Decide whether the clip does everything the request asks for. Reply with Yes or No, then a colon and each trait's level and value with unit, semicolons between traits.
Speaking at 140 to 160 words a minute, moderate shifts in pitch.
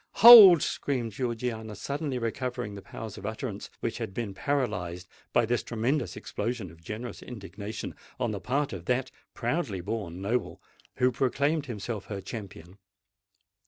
Yes: average, 145 wpm; average, 4.3 semitones